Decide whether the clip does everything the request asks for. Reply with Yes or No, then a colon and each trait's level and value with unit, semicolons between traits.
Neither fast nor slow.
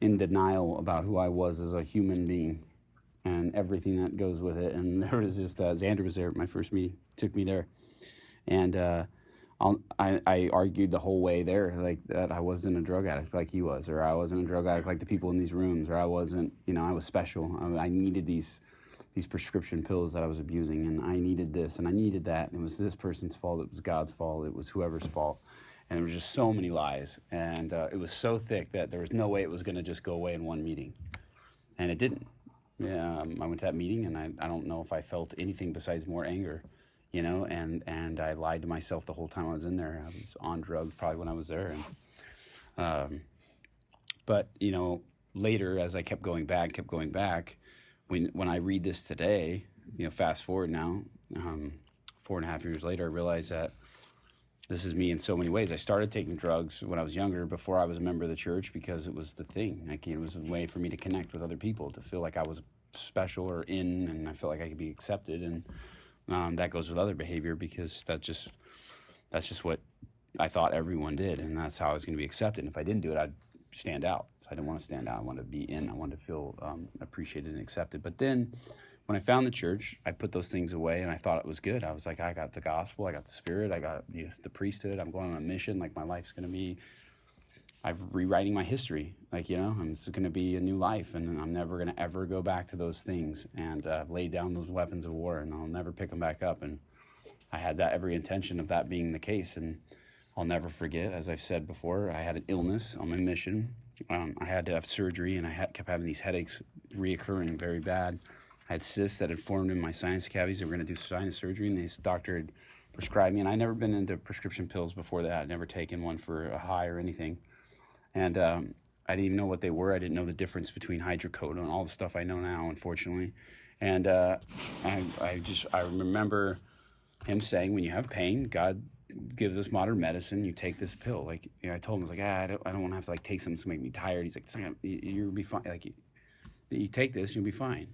No: fast, 250 wpm